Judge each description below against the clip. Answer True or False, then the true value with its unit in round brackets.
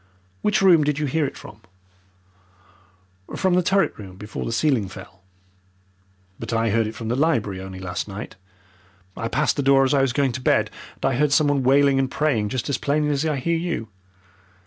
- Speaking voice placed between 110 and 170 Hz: True (135 Hz)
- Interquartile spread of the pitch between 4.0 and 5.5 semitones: True (5.2 semitones)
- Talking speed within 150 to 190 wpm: False (200 wpm)